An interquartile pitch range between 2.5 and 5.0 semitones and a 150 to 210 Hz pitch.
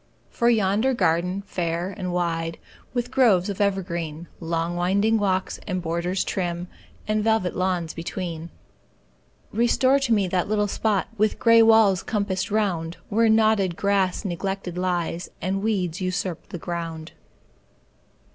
Yes: average, 3.6 semitones; medium, 185 Hz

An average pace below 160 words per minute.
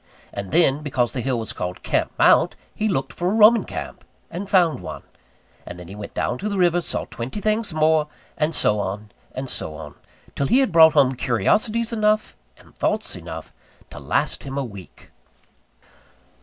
No: average, 185 wpm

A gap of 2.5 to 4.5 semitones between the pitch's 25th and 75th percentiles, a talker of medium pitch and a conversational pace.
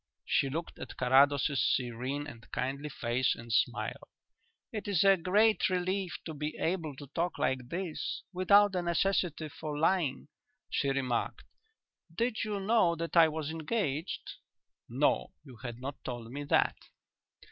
No: wide, 5.5 semitones; medium, 155 Hz; average, 145 wpm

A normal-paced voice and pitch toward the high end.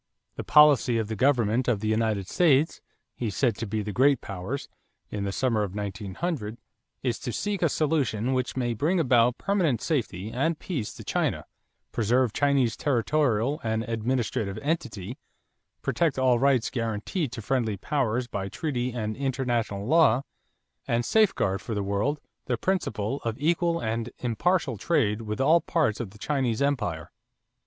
No: average, 155 wpm; low, 120 Hz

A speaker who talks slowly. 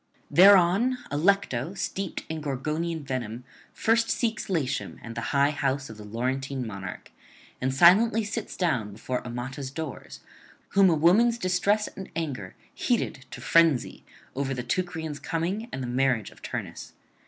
No: average, 145 wpm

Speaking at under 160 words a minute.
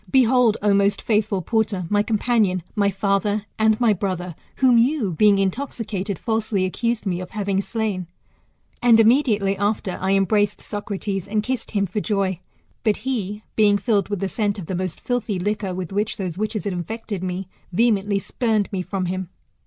No: average, 175 wpm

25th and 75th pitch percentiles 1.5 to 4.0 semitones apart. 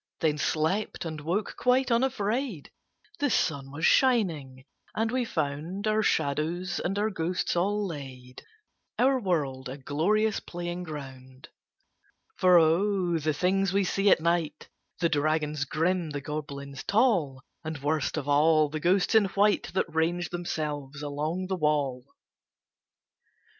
No: average, 5.0 semitones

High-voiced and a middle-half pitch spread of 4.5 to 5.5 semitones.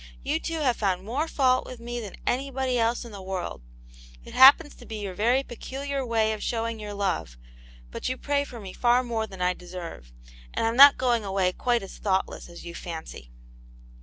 Yes: high, 230 Hz; average, 5.1 semitones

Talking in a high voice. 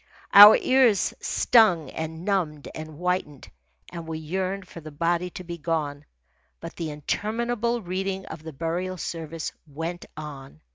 No: medium, 170 Hz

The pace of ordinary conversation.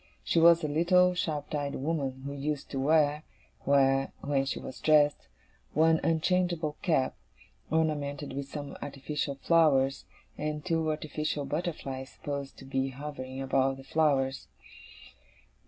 No: slow, 130 wpm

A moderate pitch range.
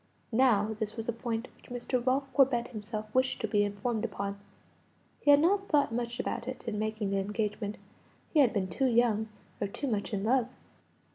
Yes: average, 3.4 semitones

